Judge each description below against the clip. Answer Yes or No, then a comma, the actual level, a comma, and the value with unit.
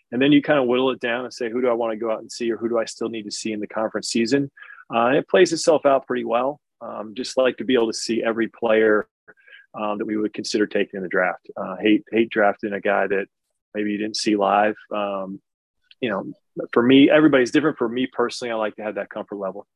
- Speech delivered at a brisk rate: Yes, fast, 265 wpm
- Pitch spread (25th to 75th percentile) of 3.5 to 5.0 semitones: No, average, 2.8 semitones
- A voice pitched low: Yes, low, 115 Hz